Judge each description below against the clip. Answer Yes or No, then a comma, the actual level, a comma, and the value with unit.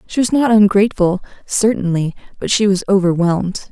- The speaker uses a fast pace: No, average, 145 wpm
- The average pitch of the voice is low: No, high, 200 Hz